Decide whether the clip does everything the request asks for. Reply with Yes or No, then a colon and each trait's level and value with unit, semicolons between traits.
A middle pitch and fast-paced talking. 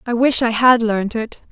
No: high, 230 Hz; fast, 240 wpm